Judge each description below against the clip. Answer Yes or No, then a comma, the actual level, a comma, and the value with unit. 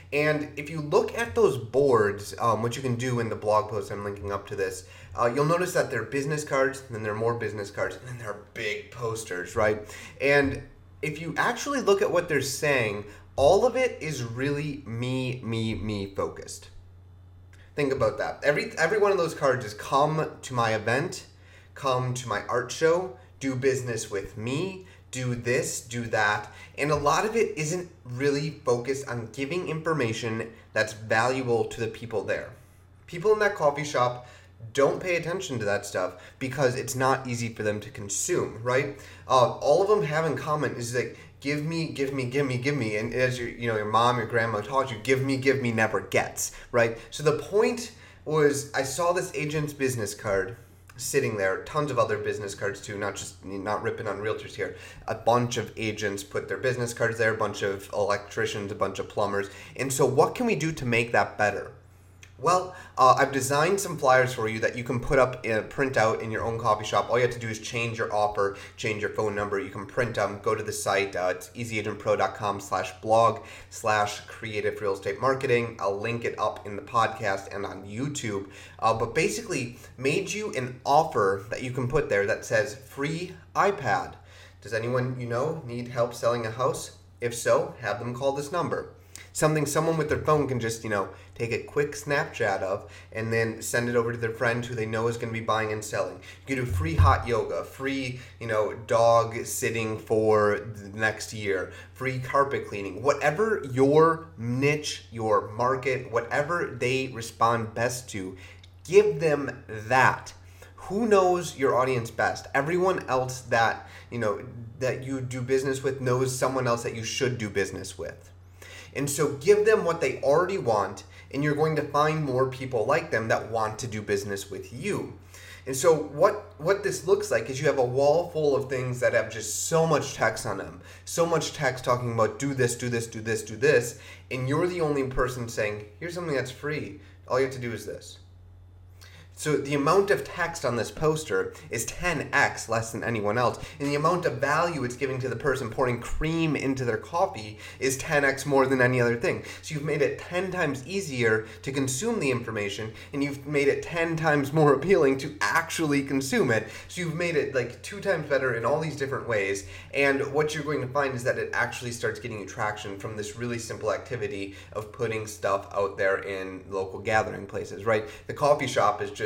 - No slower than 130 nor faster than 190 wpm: No, fast, 205 wpm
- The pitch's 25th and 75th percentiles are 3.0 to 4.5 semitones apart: No, average, 5.3 semitones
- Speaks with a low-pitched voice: Yes, low, 120 Hz